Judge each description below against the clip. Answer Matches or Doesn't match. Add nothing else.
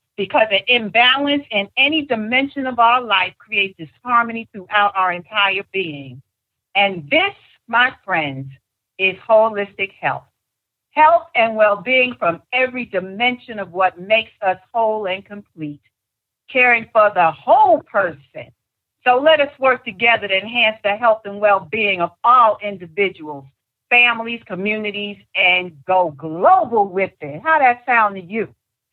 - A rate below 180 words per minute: Matches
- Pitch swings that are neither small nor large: Matches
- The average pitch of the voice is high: Matches